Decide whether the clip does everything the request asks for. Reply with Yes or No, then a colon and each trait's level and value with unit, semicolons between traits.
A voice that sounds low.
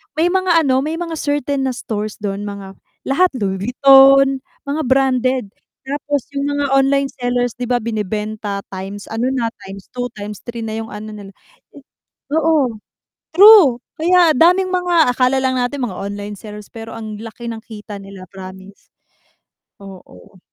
No: high, 245 Hz